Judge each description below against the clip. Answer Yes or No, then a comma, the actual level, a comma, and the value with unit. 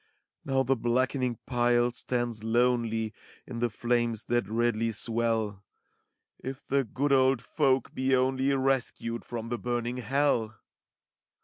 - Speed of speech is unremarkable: No, slow, 125 wpm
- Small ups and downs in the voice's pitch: Yes, narrow, 2.2 semitones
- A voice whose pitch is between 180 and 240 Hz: No, low, 120 Hz